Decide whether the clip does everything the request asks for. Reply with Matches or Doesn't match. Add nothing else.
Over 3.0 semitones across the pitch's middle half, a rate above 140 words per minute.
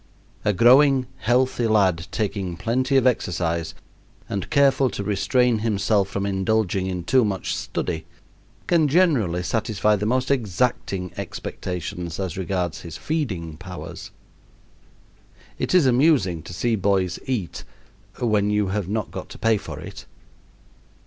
Doesn't match